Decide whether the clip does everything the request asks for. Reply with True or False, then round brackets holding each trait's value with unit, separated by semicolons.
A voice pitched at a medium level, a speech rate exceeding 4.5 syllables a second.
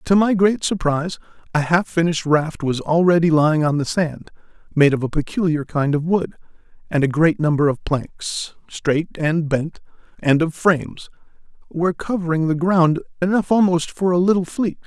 True (165 Hz; 5.0 syllables/s)